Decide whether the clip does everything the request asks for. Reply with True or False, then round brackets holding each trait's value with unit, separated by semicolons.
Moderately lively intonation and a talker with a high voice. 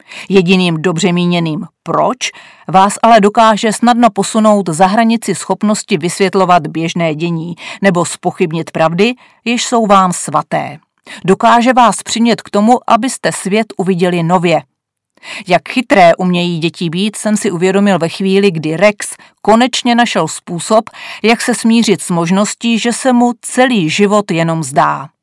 True (4.6 semitones; 195 Hz)